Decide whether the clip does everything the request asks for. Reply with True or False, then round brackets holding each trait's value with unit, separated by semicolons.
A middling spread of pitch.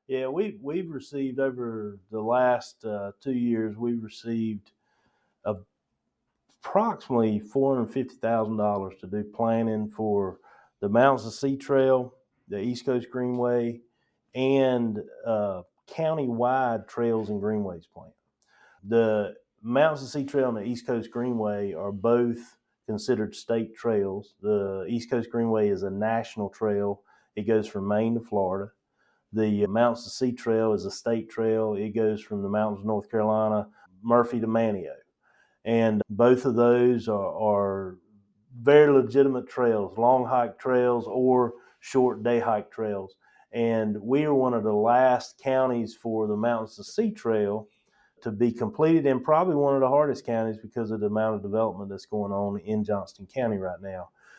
True (3.0 semitones)